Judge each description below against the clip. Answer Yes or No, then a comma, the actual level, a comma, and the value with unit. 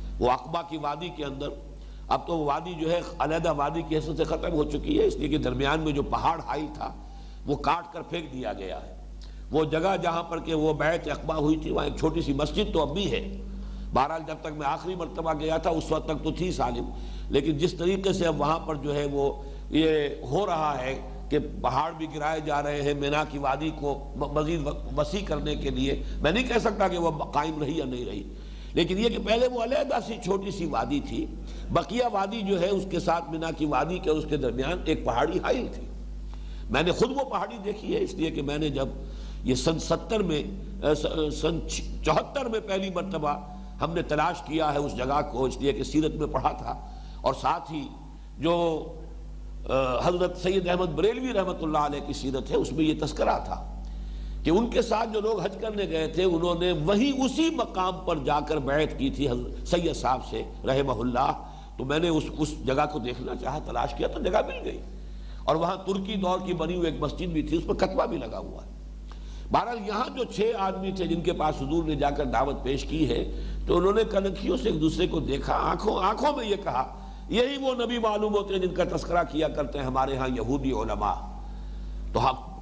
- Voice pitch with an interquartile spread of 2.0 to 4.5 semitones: Yes, average, 4.2 semitones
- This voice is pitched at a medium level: Yes, medium, 160 Hz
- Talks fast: Yes, fast, 220 wpm